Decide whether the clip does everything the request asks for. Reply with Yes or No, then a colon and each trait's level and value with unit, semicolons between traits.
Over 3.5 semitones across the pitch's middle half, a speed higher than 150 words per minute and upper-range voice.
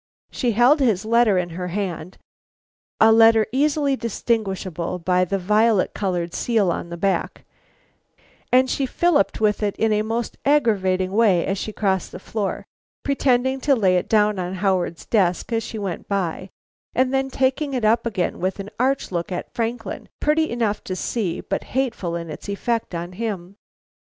Yes: average, 4.5 semitones; average, 170 wpm; high, 210 Hz